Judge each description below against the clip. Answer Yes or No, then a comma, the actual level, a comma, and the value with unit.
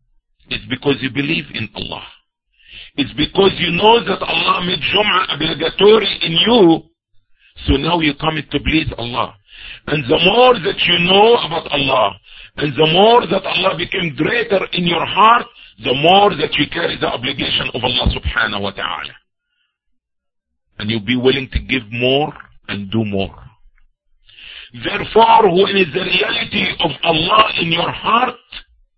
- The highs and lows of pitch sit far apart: Yes, wide, 7.0 semitones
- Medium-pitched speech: Yes, medium, 160 Hz